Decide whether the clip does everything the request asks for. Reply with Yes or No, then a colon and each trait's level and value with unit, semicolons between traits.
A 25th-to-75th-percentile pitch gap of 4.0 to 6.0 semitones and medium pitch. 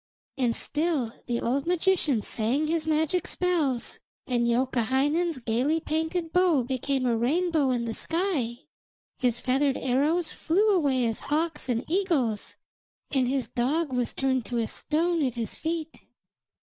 No: average, 4.9 semitones; very high, 275 Hz